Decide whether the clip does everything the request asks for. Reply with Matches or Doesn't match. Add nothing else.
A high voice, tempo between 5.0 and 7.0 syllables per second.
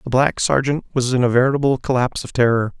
Doesn't match